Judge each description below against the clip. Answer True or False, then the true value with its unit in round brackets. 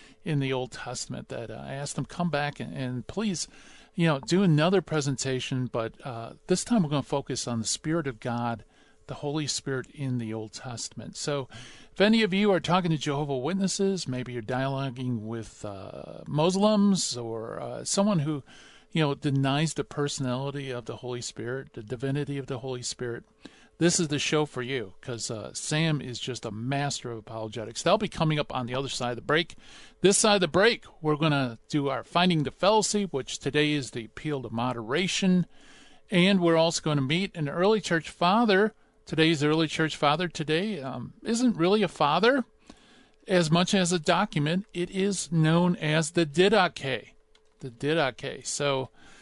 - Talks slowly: False (190 wpm)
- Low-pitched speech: False (150 Hz)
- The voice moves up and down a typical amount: False (5.7 semitones)